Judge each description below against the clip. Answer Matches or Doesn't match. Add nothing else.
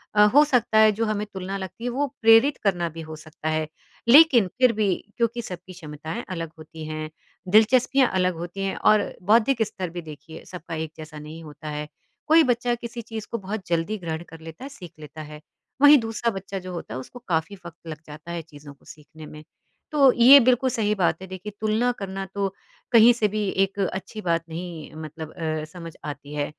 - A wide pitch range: Matches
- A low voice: Doesn't match